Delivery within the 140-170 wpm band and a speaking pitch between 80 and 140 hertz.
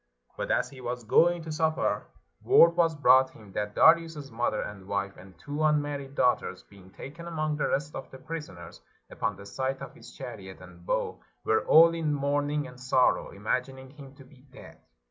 No: average, 190 wpm; low, 135 Hz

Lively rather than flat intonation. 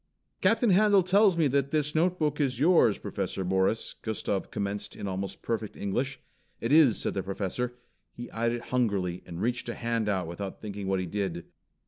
Yes: wide, 6.6 semitones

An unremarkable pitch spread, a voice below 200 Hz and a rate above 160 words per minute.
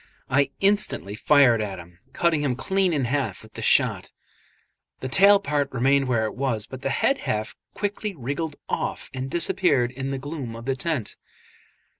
Yes: average, 4.8 semitones; low, 135 Hz; average, 175 wpm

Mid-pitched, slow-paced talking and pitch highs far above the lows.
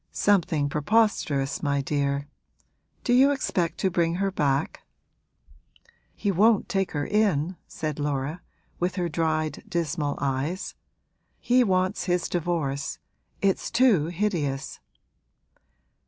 No: medium, 170 Hz; slow, 110 wpm; average, 5.0 semitones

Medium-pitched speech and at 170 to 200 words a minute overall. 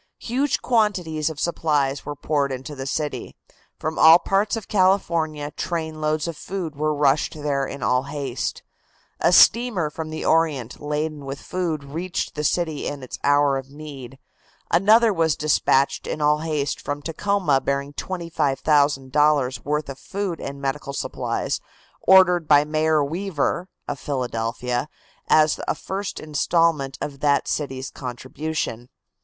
No: medium, 150 Hz; average, 140 wpm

